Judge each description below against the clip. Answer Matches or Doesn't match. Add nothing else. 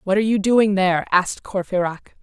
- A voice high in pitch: Matches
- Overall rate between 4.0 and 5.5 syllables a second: Doesn't match